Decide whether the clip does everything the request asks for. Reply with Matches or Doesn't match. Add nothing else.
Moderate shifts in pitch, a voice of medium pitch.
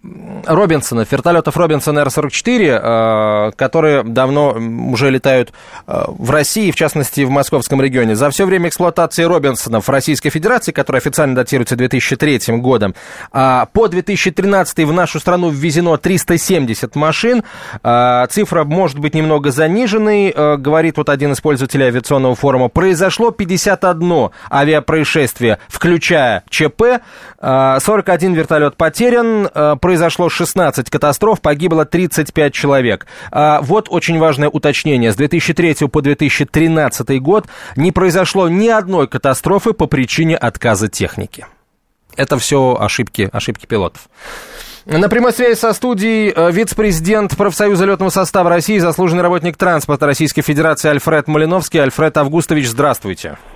Matches